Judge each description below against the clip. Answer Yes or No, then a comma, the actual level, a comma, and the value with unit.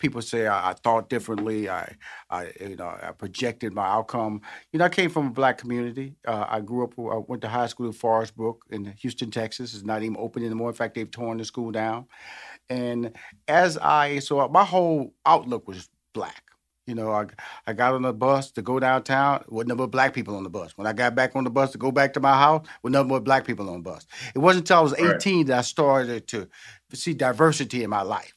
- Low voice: Yes, low, 125 Hz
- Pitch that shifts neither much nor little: Yes, average, 3.3 semitones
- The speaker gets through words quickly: Yes, fast, 240 wpm